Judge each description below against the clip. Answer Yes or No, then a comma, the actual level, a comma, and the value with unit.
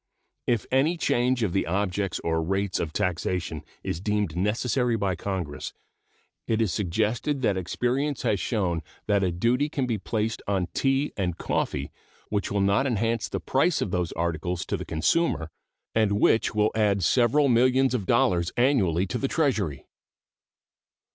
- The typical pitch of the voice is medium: No, low, 105 Hz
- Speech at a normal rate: Yes, average, 160 wpm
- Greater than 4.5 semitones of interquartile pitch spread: Yes, wide, 5.4 semitones